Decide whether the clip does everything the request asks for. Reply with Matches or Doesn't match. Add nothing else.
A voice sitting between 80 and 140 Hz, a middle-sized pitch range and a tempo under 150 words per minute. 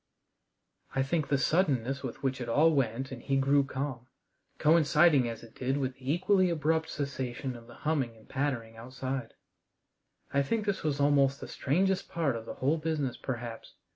Doesn't match